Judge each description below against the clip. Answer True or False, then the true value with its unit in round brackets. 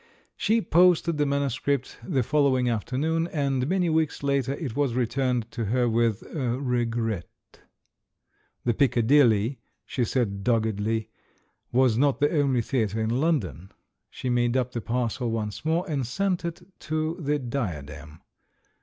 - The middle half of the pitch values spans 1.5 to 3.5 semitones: False (4.1 semitones)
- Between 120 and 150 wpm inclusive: True (145 wpm)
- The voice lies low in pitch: True (125 Hz)